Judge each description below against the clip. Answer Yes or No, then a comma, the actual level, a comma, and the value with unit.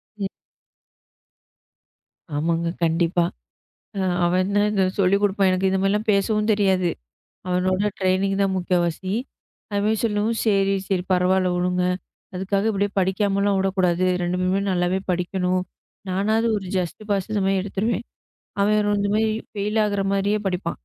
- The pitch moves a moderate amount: No, narrow, 1.9 semitones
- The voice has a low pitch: No, high, 195 Hz